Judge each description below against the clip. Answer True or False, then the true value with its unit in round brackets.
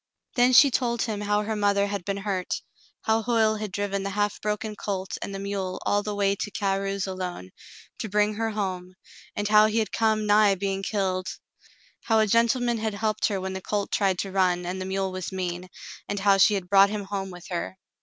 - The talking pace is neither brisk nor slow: False (215 wpm)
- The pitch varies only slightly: True (1.9 semitones)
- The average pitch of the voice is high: True (200 Hz)